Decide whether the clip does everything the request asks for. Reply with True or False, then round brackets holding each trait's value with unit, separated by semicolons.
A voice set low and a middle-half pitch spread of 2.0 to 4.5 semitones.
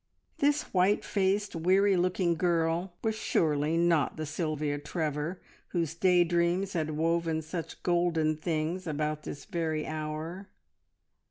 False (165 Hz; 2.7 semitones)